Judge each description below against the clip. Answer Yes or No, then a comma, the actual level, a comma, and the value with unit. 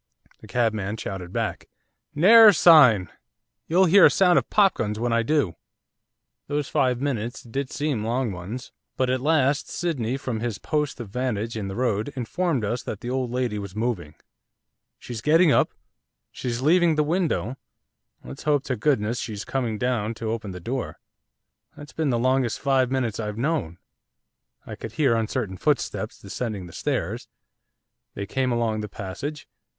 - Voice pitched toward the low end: Yes, low, 125 Hz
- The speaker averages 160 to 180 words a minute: Yes, average, 165 wpm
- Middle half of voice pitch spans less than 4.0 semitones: No, average, 4.8 semitones